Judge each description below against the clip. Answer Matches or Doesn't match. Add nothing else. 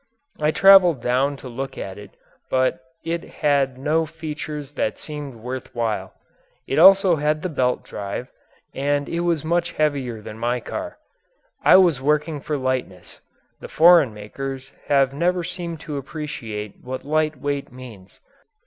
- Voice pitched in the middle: Matches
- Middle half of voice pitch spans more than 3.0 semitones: Matches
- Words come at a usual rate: Matches